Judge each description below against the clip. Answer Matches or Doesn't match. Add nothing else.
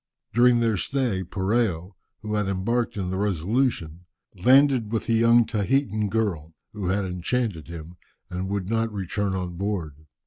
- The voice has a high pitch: Doesn't match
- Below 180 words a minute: Matches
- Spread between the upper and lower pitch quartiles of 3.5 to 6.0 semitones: Matches